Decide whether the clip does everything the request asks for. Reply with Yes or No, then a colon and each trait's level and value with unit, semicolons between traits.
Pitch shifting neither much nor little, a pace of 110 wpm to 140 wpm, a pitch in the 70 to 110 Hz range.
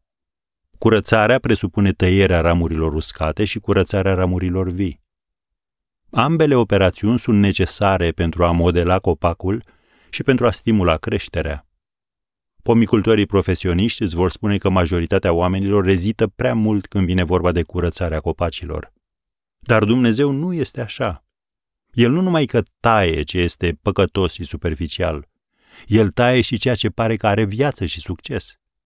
Yes: average, 4.6 semitones; average, 135 wpm; very low, 95 Hz